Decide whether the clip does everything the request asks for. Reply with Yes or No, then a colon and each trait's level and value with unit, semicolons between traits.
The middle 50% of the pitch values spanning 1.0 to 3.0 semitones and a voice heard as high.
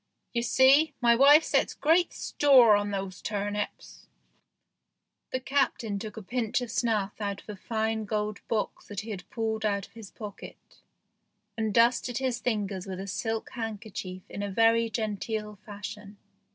Yes: narrow, 2.4 semitones; high, 220 Hz